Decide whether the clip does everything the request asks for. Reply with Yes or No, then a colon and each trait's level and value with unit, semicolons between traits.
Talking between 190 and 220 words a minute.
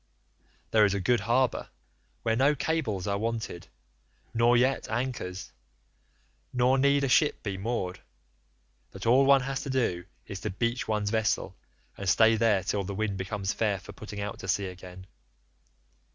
No: average, 165 wpm